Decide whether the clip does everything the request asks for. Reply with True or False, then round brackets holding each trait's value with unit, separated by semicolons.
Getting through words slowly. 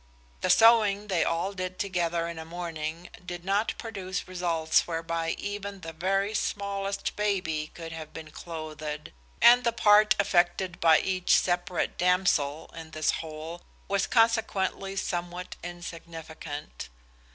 True (130 wpm)